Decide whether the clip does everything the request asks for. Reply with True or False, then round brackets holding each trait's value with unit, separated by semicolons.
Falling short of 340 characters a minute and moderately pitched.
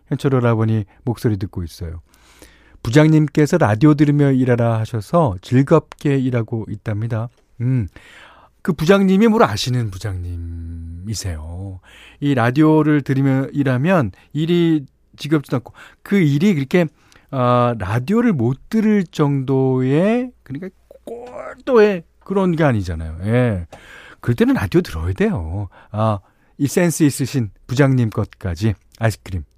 False (280 characters per minute; 125 Hz)